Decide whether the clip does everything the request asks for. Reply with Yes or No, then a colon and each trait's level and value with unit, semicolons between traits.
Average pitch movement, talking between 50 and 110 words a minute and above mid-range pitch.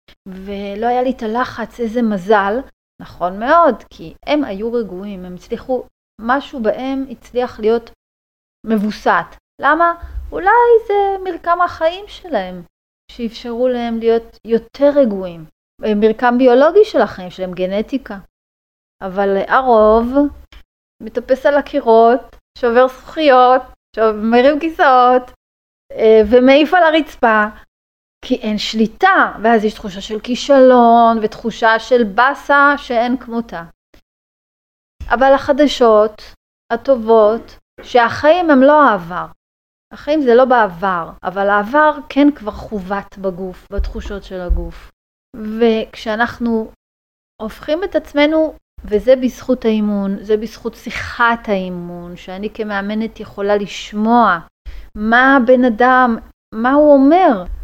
Yes: average, 4.1 semitones; average, 105 wpm; high, 230 Hz